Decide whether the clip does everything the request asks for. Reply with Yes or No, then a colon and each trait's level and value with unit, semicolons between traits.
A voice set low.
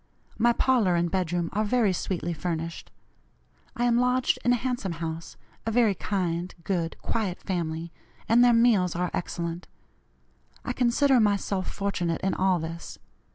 No: high, 190 Hz